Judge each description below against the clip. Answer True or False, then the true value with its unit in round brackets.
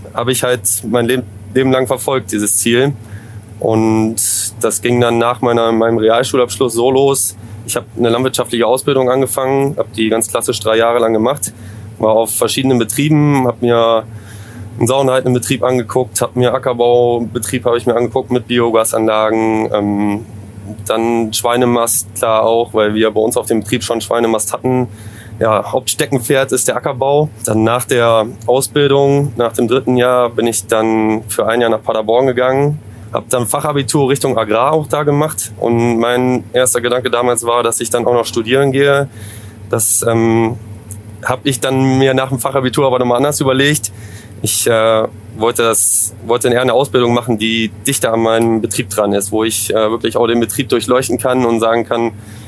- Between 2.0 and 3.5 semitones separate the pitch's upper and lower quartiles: True (2.6 semitones)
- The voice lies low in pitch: True (120 Hz)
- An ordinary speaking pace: True (175 wpm)